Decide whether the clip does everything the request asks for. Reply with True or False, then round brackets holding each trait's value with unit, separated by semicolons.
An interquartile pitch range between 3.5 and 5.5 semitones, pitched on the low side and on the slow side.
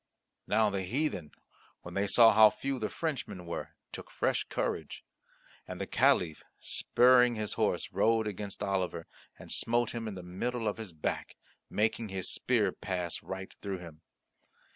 False (4.1 semitones; 105 Hz; 160 wpm)